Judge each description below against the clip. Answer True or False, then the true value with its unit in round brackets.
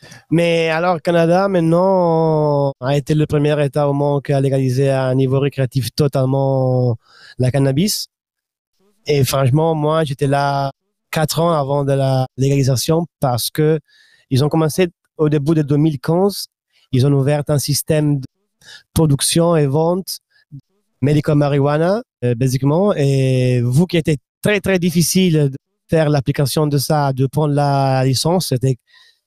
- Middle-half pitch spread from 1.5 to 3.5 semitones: True (3.2 semitones)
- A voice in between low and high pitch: True (150 Hz)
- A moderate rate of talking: False (140 wpm)